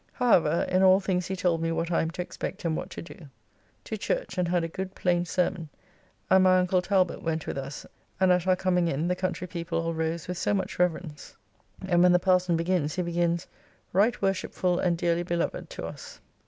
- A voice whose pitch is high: No, medium, 180 Hz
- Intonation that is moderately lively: No, narrow, 1.8 semitones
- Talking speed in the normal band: No, fast, 215 wpm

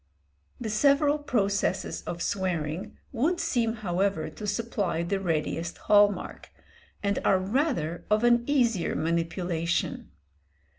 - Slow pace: Yes, slow, 115 wpm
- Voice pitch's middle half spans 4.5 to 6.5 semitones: Yes, wide, 5.5 semitones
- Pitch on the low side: No, high, 200 Hz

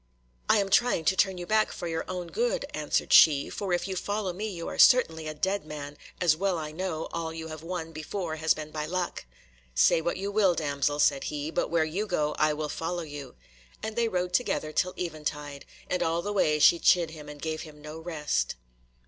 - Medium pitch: Yes, medium, 165 Hz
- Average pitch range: Yes, average, 3.3 semitones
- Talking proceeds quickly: Yes, fast, 220 wpm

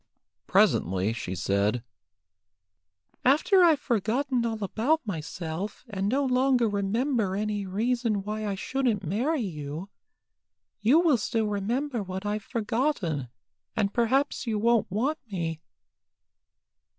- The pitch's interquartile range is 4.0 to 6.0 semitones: Yes, average, 4.7 semitones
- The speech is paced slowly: Yes, slow, 115 wpm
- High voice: Yes, high, 215 Hz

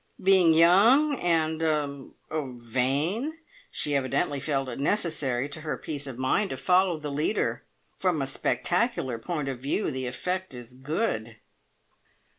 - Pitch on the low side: No, medium, 150 Hz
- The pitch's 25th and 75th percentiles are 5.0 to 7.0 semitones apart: Yes, average, 5.3 semitones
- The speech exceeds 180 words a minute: No, average, 140 wpm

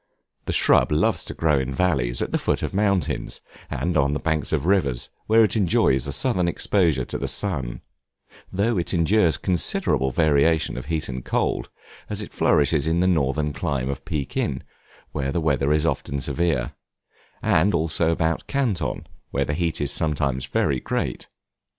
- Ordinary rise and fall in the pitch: Yes, average, 4.1 semitones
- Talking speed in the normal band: Yes, average, 170 wpm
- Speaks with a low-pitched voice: Yes, very low, 80 Hz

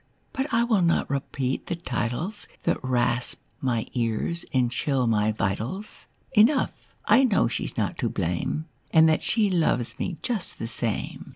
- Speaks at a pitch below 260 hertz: Yes, medium, 140 Hz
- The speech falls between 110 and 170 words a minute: Yes, average, 160 wpm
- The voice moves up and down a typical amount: No, wide, 8.6 semitones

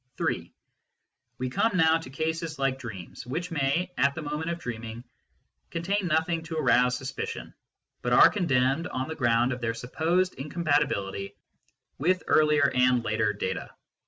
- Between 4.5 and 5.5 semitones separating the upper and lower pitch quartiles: Yes, average, 4.8 semitones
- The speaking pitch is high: No, medium, 140 Hz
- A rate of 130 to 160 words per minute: Yes, average, 155 wpm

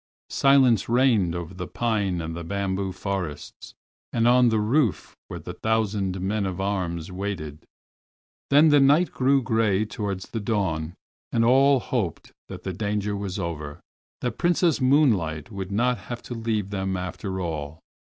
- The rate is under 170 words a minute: Yes, average, 155 wpm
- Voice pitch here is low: Yes, low, 100 Hz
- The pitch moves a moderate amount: Yes, average, 4.6 semitones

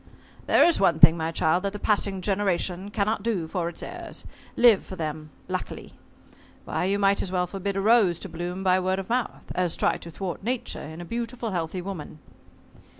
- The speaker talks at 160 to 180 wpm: No, average, 200 wpm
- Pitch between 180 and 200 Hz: Yes, high, 190 Hz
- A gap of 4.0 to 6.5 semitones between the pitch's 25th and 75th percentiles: No, average, 2.8 semitones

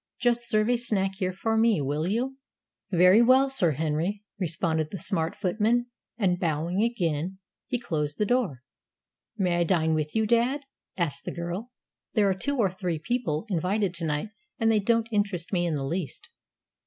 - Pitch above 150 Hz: Yes, high, 190 Hz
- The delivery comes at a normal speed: Yes, average, 180 wpm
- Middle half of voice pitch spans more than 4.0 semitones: Yes, average, 5.3 semitones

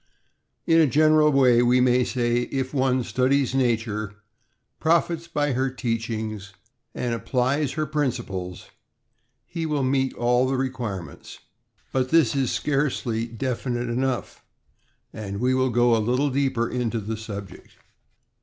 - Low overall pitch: Yes, low, 125 Hz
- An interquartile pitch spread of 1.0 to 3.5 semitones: Yes, average, 2.8 semitones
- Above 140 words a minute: No, slow, 135 wpm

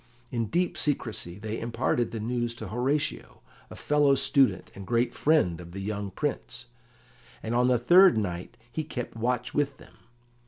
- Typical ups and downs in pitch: Yes, average, 4.3 semitones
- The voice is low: Yes, low, 120 Hz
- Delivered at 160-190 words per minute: Yes, average, 165 wpm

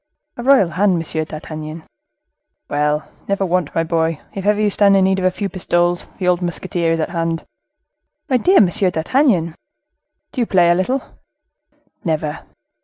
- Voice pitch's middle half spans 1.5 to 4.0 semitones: Yes, average, 3.3 semitones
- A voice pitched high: No, medium, 175 Hz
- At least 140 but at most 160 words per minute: No, average, 170 wpm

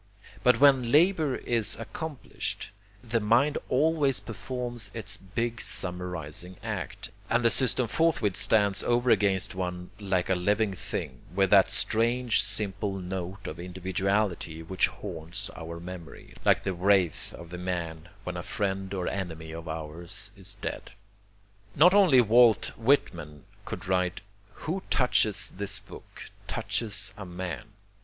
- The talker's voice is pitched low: Yes, low, 100 Hz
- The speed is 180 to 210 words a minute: No, average, 140 wpm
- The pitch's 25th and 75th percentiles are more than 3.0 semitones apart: Yes, average, 4.7 semitones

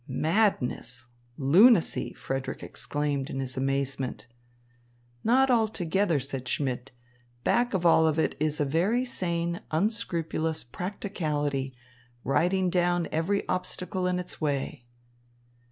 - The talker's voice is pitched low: No, medium, 160 Hz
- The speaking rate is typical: No, slow, 105 wpm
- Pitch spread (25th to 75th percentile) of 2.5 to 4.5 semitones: No, average, 5.3 semitones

